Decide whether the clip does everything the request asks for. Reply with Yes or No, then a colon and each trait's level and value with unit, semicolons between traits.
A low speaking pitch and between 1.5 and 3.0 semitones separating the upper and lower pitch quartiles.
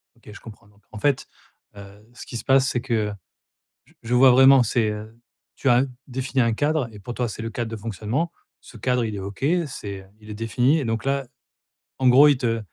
No: low, 120 Hz; average, 3.6 semitones